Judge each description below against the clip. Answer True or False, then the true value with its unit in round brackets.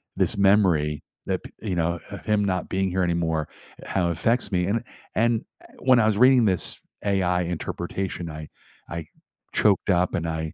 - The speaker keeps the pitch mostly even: False (3.4 semitones)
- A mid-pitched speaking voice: False (90 Hz)